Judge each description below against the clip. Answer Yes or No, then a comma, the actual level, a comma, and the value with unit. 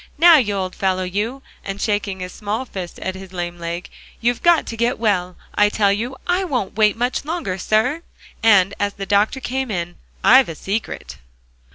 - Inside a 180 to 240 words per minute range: Yes, average, 190 wpm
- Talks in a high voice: Yes, high, 205 Hz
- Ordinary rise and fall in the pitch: Yes, average, 4.7 semitones